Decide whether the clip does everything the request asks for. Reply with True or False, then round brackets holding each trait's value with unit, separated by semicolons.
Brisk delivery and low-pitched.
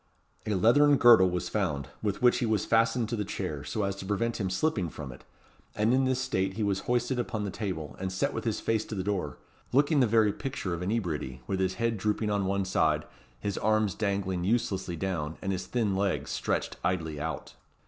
True (215 wpm; 100 Hz)